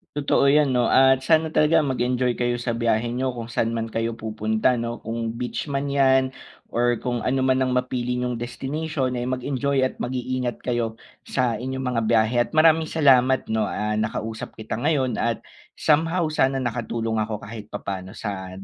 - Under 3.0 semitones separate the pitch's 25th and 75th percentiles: Yes, narrow, 2.6 semitones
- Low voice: Yes, low, 125 Hz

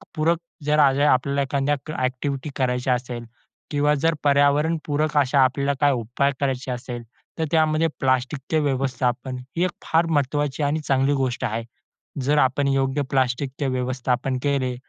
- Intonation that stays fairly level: Yes, narrow, 2.3 semitones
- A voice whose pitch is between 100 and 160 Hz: Yes, low, 135 Hz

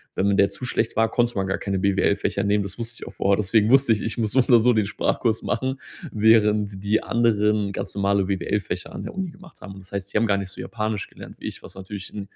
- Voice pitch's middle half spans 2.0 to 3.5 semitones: Yes, narrow, 2.5 semitones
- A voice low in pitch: Yes, low, 105 Hz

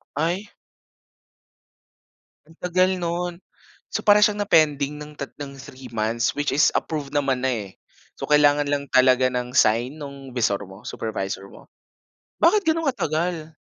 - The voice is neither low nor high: Yes, medium, 145 Hz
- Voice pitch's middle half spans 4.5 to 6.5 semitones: Yes, average, 4.9 semitones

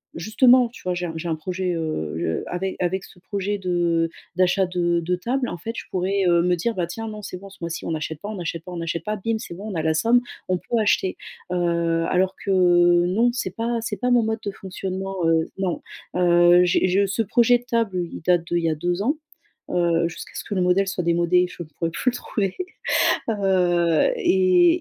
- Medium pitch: Yes, medium, 180 Hz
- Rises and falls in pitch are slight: No, average, 3.3 semitones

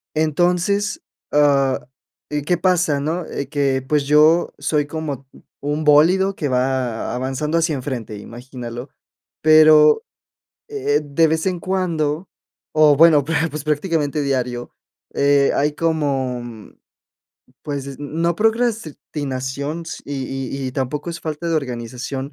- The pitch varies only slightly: No, average, 3.2 semitones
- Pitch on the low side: No, medium, 150 Hz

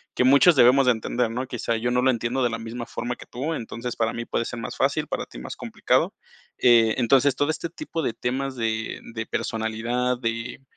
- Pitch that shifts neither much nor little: No, narrow, 2.2 semitones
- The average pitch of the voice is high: No, low, 120 Hz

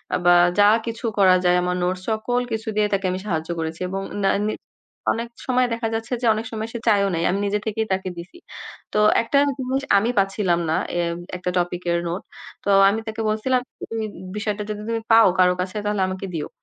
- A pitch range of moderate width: Yes, average, 3.5 semitones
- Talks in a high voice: Yes, high, 205 Hz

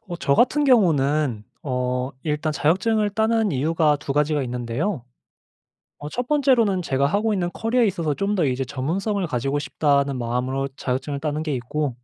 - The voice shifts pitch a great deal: Yes, wide, 6.7 semitones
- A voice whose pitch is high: No, medium, 150 Hz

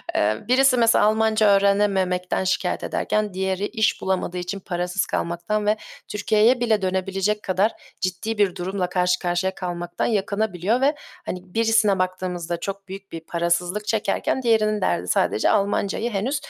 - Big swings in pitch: No, average, 2.9 semitones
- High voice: Yes, high, 195 Hz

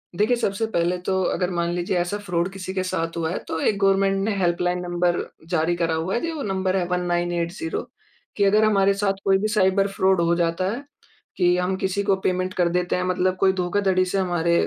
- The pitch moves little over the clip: Yes, narrow, 2.0 semitones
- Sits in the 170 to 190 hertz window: Yes, medium, 185 Hz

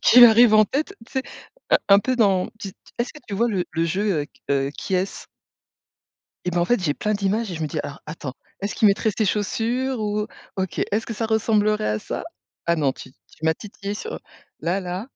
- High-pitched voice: Yes, high, 205 Hz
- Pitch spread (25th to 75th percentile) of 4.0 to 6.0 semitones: Yes, average, 4.3 semitones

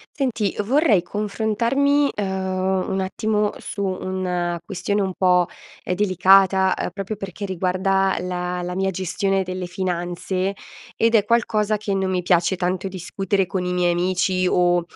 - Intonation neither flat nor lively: No, narrow, 2.2 semitones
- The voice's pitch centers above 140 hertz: Yes, high, 190 Hz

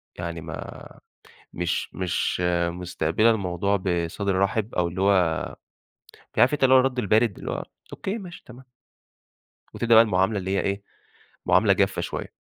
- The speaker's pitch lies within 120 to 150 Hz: No, low, 100 Hz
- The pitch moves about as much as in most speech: Yes, average, 4.4 semitones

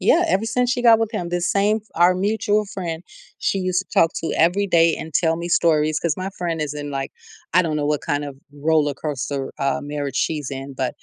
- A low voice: No, medium, 165 Hz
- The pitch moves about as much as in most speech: Yes, average, 4.4 semitones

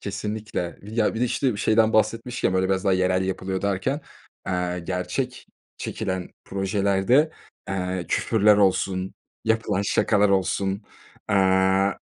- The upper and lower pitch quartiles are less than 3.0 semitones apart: Yes, narrow, 2.6 semitones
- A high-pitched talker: No, low, 100 Hz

